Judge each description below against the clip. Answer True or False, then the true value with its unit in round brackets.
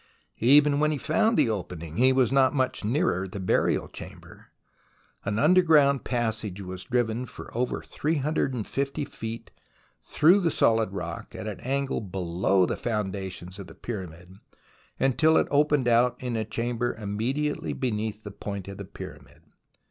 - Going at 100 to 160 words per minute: True (155 wpm)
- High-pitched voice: False (115 Hz)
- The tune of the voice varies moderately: False (5.7 semitones)